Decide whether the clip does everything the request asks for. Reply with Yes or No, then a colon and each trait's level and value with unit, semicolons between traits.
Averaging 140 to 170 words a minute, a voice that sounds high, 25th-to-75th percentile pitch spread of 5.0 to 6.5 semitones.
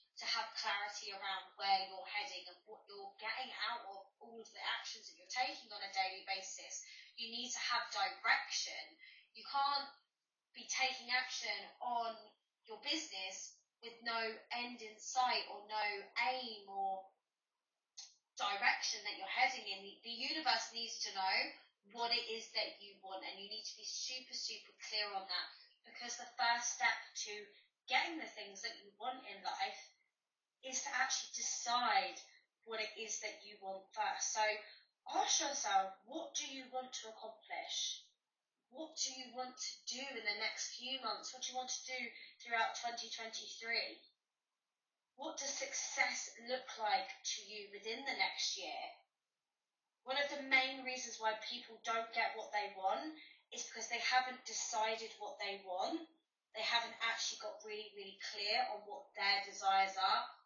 No: average, 165 wpm; high, 230 Hz; average, 3.9 semitones